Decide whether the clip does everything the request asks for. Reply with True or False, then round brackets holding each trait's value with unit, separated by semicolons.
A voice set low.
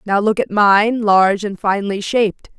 False (205 Hz)